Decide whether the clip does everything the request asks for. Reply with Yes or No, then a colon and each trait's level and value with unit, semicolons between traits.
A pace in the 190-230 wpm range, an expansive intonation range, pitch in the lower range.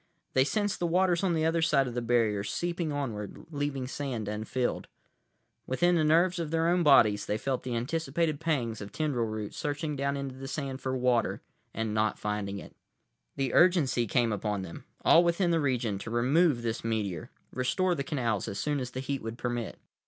Yes: average, 195 wpm; wide, 5.8 semitones; low, 130 Hz